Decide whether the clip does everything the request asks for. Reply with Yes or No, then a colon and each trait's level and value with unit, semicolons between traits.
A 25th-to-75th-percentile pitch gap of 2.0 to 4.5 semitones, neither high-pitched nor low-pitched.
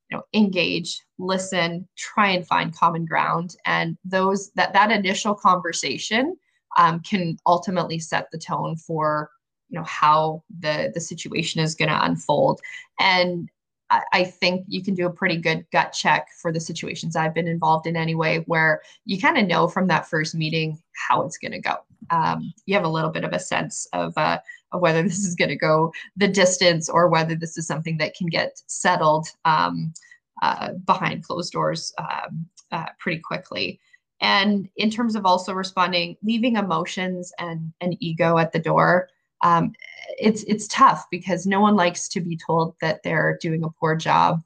Yes: average, 3.0 semitones; medium, 175 Hz